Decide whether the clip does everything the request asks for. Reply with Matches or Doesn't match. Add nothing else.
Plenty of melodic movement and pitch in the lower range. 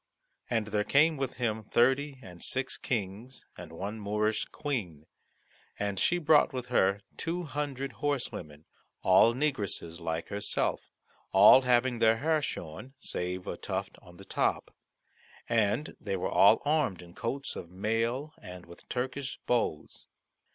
Matches